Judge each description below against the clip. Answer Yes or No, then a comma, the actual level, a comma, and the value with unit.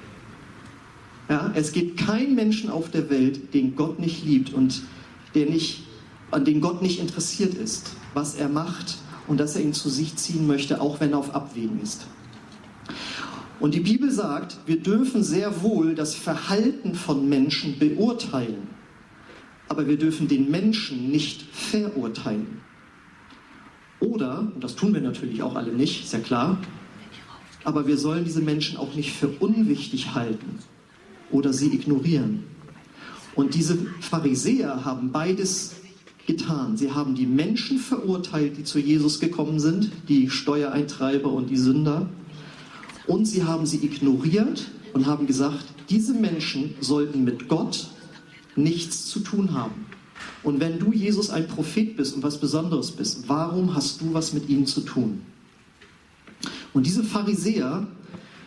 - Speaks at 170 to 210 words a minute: No, average, 145 wpm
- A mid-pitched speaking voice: Yes, medium, 155 Hz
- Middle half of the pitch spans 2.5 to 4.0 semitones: No, average, 4.8 semitones